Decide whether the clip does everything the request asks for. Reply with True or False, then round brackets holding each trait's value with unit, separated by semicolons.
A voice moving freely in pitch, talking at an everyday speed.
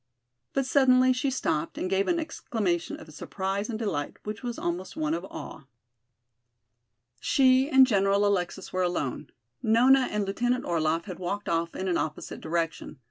True (6.7 semitones; 160 wpm)